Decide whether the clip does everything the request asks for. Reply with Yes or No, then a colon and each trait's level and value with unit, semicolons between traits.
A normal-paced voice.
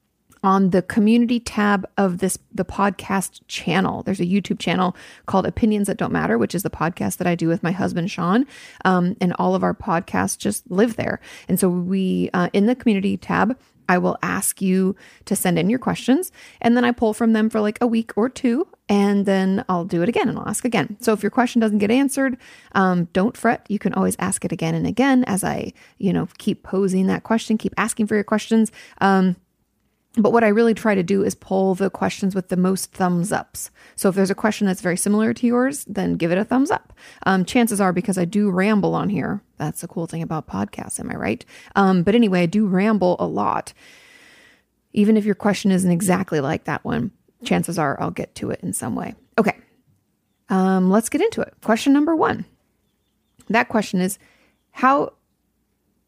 No: fast, 210 wpm